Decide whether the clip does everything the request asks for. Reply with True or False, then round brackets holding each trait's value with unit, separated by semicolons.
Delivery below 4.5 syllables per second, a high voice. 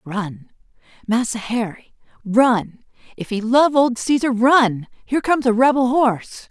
True (4.1 syllables/s; 235 Hz)